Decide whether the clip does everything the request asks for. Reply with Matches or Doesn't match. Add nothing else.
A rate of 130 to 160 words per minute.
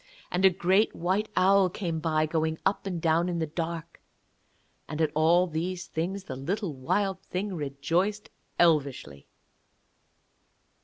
Matches